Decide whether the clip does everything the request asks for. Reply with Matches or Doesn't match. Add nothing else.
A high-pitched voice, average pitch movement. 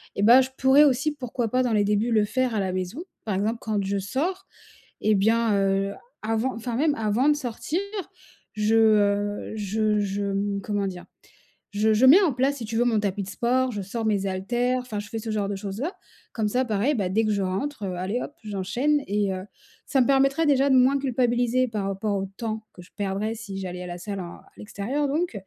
Matches